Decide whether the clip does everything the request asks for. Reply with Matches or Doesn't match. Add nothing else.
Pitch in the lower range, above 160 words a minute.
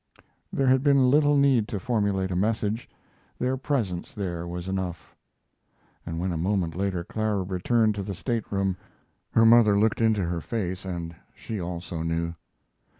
Doesn't match